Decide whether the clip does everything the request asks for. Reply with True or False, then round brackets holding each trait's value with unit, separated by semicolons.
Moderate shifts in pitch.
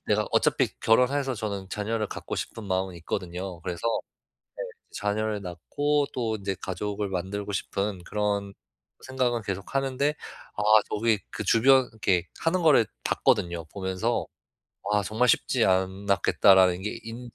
True (3.6 semitones)